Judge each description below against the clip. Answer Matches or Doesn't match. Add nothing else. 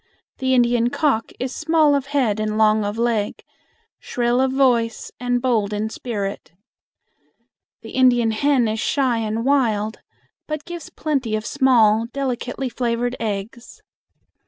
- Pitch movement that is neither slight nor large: Matches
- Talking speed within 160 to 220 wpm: Doesn't match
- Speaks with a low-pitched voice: Doesn't match